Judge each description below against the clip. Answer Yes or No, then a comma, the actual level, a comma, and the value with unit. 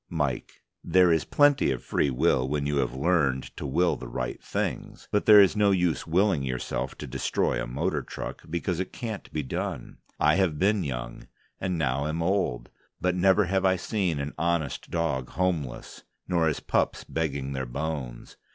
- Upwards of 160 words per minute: Yes, average, 180 wpm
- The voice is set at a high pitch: No, very low, 80 Hz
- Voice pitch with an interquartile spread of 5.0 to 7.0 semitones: Yes, wide, 5.4 semitones